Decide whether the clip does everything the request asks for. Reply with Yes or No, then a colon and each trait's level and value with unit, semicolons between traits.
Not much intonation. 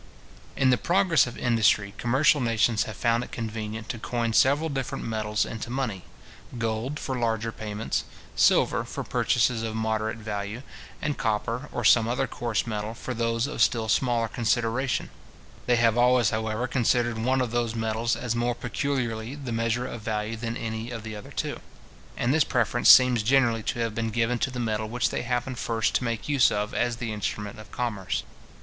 Yes: narrow, 1.9 semitones